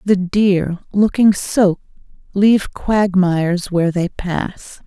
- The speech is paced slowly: Yes, slow, 110 wpm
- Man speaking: No, female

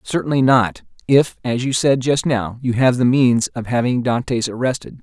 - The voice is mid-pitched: No, low, 125 Hz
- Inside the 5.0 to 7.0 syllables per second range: No, 4.8 syllables/s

